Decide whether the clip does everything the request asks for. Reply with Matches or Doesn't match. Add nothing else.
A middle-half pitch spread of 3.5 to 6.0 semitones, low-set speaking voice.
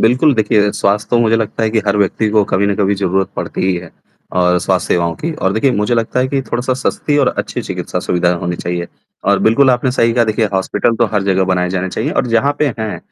Matches